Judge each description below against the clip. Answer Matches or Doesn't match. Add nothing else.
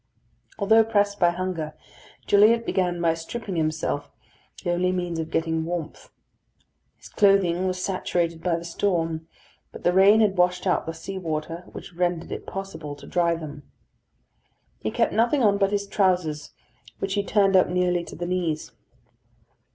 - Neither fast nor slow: Matches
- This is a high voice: Doesn't match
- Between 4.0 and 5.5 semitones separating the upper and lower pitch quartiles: Doesn't match